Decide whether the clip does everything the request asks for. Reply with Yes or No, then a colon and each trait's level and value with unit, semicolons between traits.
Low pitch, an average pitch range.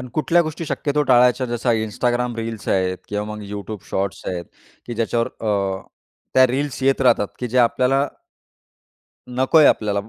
Yes: low, 120 Hz; average, 3.9 semitones